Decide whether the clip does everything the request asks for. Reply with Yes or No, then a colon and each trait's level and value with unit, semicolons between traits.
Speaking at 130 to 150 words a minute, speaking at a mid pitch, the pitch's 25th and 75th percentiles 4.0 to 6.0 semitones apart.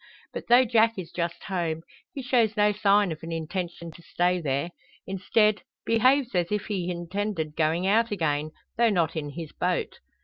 No: average, 175 wpm; medium, 180 Hz; average, 4.4 semitones